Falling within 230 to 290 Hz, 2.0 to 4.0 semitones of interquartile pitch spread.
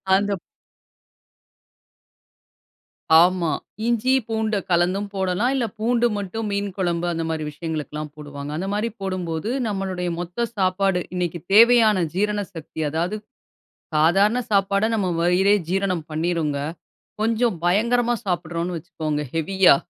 No: medium, 185 Hz; average, 3.7 semitones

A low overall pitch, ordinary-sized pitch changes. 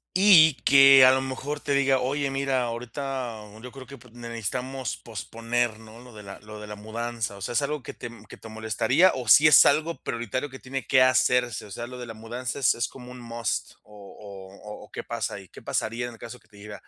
Yes: low, 120 Hz; average, 3.2 semitones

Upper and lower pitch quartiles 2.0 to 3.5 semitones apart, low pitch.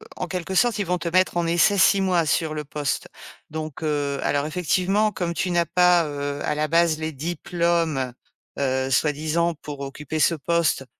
No: average, 2.9 semitones; medium, 160 Hz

